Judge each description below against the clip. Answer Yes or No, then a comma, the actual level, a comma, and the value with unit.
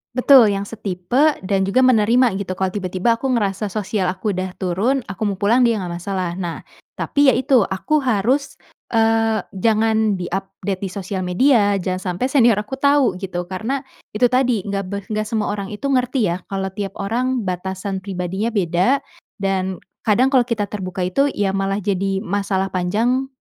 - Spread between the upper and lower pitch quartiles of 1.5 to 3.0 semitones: No, average, 3.8 semitones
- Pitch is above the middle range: Yes, high, 200 Hz